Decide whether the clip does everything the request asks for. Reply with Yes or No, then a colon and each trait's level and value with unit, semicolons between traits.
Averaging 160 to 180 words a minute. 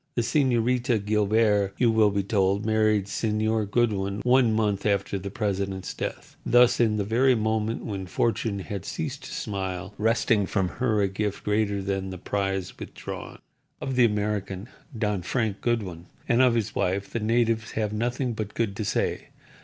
Yes: average, 170 wpm